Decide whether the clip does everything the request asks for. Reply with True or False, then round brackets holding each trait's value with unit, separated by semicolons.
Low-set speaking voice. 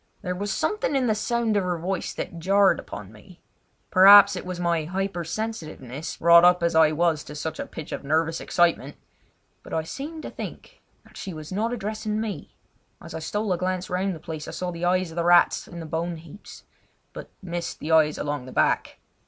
False (175 Hz)